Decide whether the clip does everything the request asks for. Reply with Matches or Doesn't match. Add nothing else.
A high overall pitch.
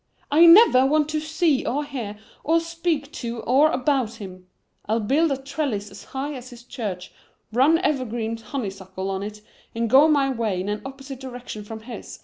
Matches